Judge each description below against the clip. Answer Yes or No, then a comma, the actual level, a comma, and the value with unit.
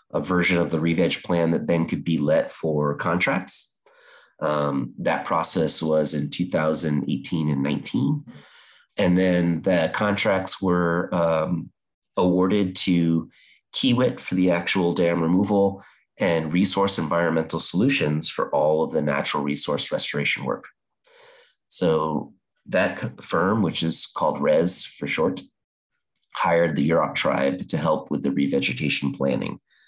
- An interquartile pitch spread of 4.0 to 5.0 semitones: No, average, 3.0 semitones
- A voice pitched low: Yes, very low, 85 Hz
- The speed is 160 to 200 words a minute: No, slow, 135 wpm